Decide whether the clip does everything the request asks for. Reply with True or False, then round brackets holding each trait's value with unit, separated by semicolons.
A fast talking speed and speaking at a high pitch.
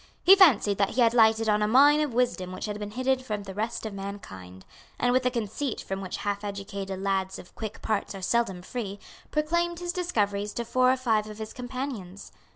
True (215 wpm; 215 Hz)